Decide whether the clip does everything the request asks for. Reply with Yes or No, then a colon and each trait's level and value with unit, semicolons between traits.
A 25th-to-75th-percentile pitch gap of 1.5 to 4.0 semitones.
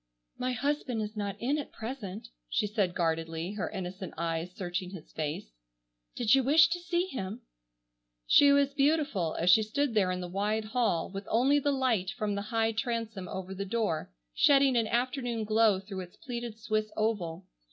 No: average, 5.1 semitones